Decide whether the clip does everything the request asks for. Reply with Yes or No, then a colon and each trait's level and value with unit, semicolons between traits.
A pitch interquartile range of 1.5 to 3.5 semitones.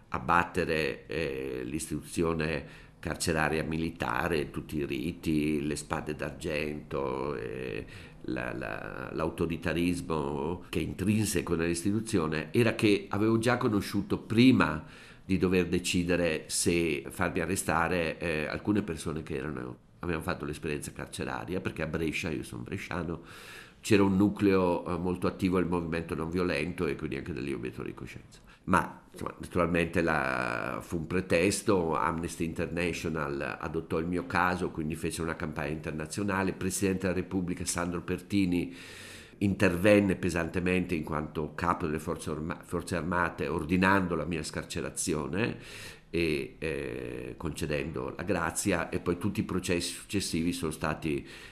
Yes: narrow, 2.6 semitones